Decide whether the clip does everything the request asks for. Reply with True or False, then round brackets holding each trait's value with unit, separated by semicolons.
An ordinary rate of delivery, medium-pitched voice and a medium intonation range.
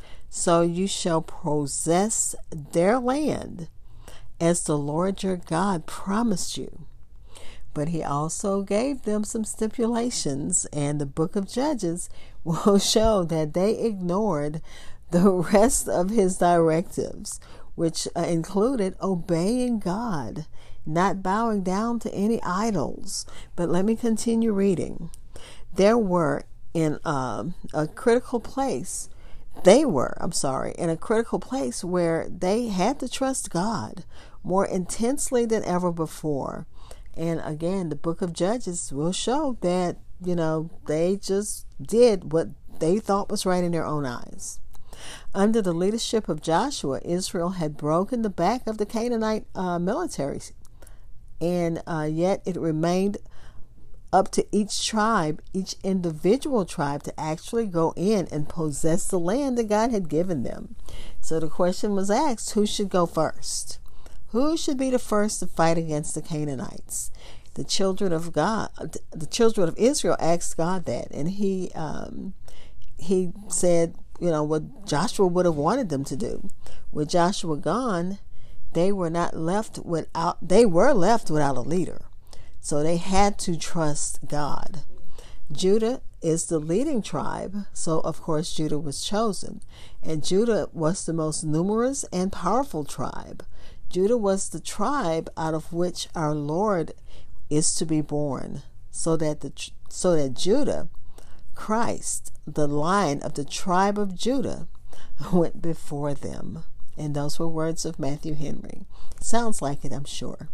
True (145 wpm; 175 Hz; 4.8 semitones)